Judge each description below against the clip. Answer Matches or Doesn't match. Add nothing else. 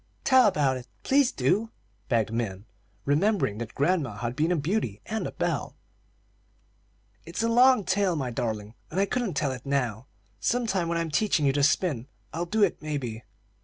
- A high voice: Doesn't match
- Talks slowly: Doesn't match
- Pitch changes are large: Matches